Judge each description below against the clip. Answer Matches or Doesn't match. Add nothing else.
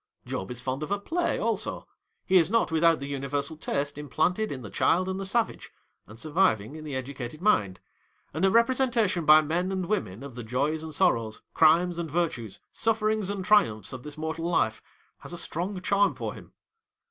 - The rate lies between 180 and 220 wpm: Matches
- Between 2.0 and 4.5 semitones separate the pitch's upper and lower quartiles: Doesn't match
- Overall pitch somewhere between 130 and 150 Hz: Doesn't match